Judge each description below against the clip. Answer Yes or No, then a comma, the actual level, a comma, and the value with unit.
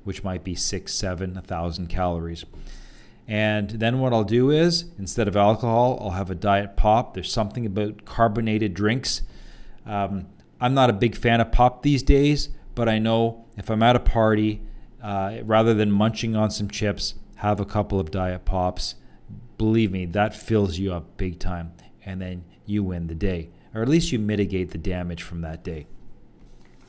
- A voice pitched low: Yes, low, 105 Hz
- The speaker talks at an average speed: Yes, average, 185 wpm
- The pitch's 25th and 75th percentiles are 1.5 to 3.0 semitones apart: No, average, 3.5 semitones